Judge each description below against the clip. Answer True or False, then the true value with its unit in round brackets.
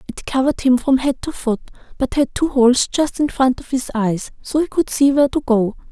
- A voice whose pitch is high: True (260 Hz)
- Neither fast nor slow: False (245 wpm)